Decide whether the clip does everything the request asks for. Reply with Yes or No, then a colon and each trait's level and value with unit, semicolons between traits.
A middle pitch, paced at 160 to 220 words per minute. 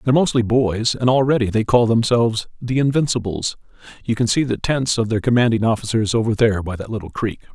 No: low, 115 Hz; average, 200 wpm